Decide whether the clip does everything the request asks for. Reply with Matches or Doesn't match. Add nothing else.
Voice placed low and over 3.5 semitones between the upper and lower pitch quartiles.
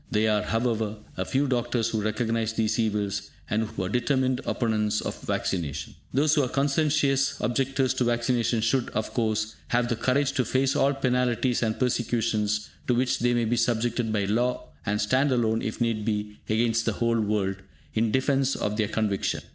Doesn't match